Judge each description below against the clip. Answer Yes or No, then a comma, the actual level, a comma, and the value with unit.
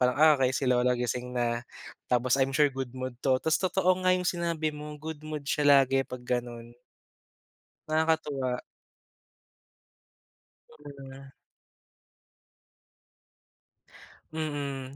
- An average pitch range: Yes, average, 3.5 semitones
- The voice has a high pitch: No, low, 135 Hz